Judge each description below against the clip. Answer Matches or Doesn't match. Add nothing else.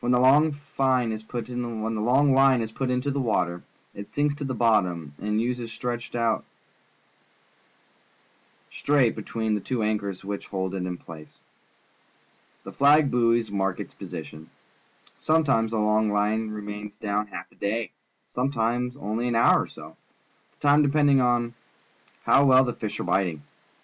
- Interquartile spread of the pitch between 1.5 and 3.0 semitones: Doesn't match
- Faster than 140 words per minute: Matches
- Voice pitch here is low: Matches